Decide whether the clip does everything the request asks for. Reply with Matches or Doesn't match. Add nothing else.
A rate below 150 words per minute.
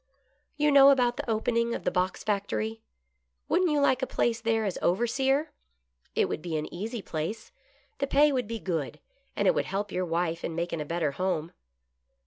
Doesn't match